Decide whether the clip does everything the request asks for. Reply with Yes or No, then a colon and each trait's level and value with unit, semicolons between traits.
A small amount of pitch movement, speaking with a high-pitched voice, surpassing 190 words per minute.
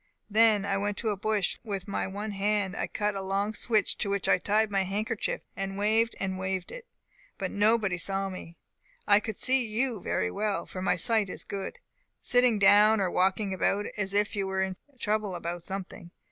Yes: narrow, 2.0 semitones; high, 200 Hz; average, 200 wpm